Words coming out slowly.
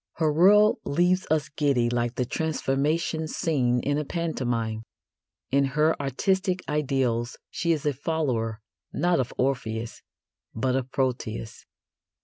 Yes: slow, 125 wpm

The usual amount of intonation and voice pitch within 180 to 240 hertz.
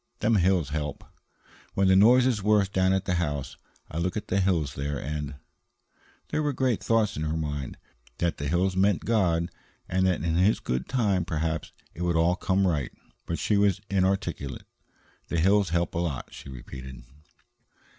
No: average, 4.1 semitones; very low, 90 Hz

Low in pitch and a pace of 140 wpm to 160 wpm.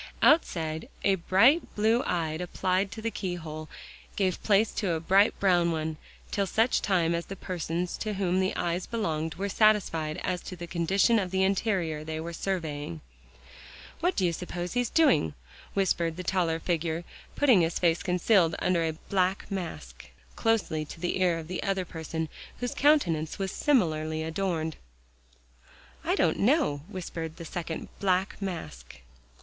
No: medium, 180 Hz; average, 155 wpm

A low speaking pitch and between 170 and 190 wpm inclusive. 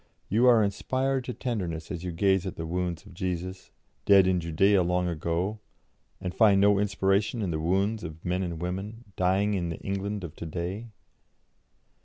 Yes: very low, 95 Hz; average, 180 wpm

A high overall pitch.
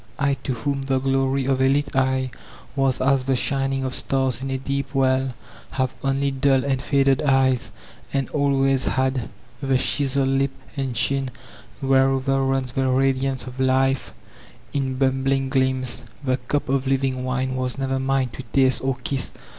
No: low, 135 Hz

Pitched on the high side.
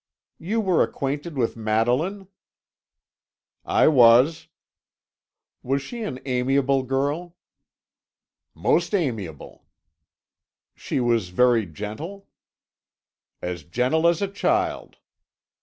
No: low, 135 Hz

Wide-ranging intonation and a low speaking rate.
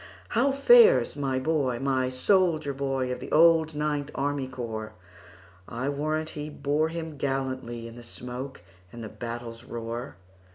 No: average, 4.3 semitones; slow, 125 wpm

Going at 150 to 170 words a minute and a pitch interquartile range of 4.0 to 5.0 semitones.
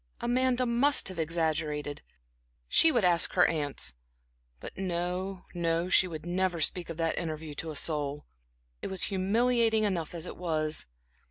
No: average, 155 wpm; average, 3.4 semitones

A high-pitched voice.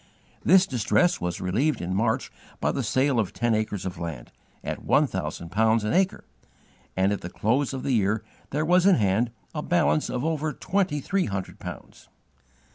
No: low, 115 Hz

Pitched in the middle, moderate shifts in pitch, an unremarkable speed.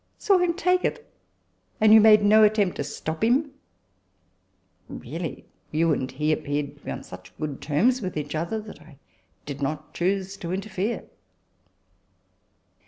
No: medium, 170 Hz; wide, 6.9 semitones; average, 170 wpm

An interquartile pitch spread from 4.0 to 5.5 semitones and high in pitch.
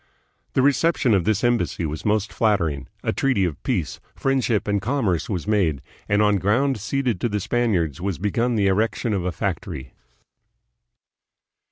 No: average, 4.9 semitones; low, 105 Hz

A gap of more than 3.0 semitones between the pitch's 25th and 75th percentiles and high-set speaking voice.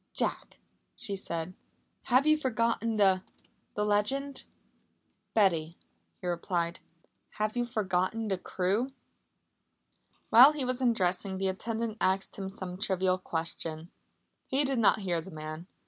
Yes: average, 4.3 semitones; high, 195 Hz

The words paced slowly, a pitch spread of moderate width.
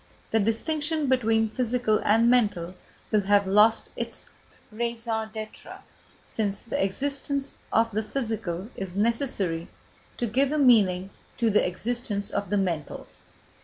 Yes: slow, 130 wpm; average, 3.3 semitones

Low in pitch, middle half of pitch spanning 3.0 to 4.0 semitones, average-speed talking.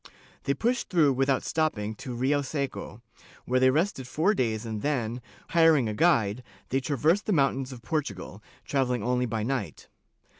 No: low, 130 Hz; average, 4.5 semitones; average, 160 wpm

